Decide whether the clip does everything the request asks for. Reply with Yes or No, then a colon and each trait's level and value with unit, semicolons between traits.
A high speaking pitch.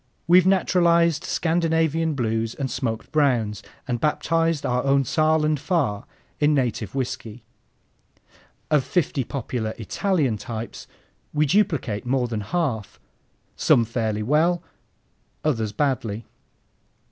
No: low, 135 Hz